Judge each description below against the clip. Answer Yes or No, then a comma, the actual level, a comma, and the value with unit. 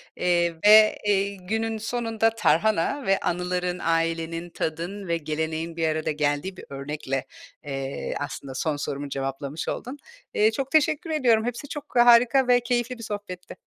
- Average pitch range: No, wide, 6.2 semitones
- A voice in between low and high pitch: Yes, medium, 180 Hz